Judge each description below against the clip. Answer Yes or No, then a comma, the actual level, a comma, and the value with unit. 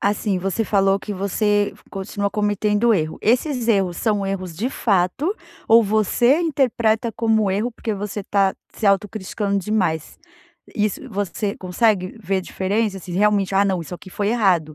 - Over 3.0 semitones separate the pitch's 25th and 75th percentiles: No, narrow, 2.4 semitones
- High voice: Yes, high, 205 Hz